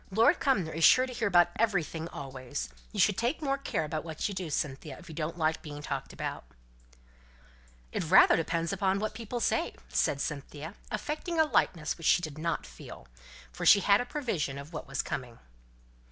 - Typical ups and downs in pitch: No, wide, 6.1 semitones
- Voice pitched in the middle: Yes, medium, 170 Hz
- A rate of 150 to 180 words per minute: No, average, 195 wpm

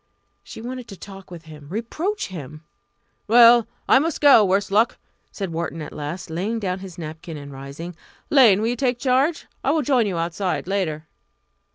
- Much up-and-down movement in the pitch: Yes, wide, 6.6 semitones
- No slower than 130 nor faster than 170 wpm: No, average, 180 wpm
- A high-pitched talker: Yes, high, 195 Hz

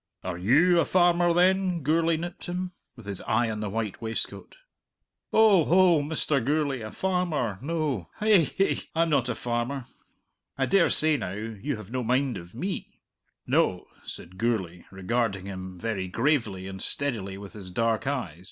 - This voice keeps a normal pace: Yes, average, 165 wpm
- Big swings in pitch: Yes, wide, 8.3 semitones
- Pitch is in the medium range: No, low, 125 Hz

